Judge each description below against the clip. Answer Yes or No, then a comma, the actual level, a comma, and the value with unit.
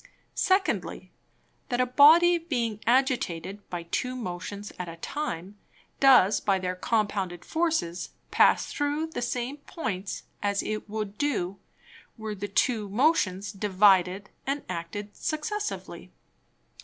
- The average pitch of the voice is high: Yes, high, 210 Hz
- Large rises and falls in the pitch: Yes, wide, 6.5 semitones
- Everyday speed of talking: No, slow, 120 wpm